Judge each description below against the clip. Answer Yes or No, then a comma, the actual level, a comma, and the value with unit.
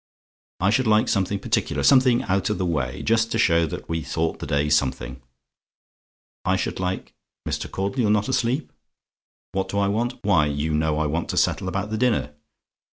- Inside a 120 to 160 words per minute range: No, average, 190 wpm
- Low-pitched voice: Yes, very low, 95 Hz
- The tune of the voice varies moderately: No, wide, 5.7 semitones